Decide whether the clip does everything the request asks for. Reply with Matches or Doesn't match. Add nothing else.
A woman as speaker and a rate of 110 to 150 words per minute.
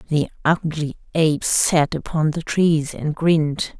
Matches